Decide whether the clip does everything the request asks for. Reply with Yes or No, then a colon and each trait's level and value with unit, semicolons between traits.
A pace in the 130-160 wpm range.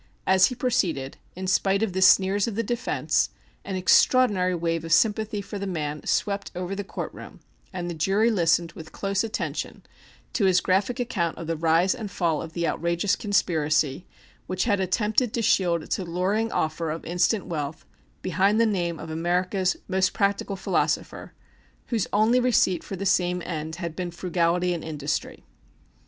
No: average, 175 wpm